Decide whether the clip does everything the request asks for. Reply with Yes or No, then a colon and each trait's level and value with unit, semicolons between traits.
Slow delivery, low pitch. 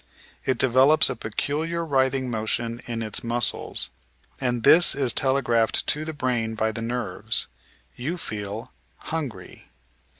Yes: slow, 130 wpm; low, 125 Hz